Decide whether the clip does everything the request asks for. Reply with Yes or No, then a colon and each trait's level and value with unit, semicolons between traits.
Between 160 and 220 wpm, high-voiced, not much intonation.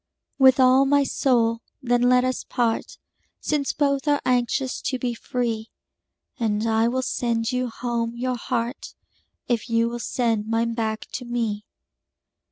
No: average, 150 wpm; high, 240 Hz; narrow, 1.9 semitones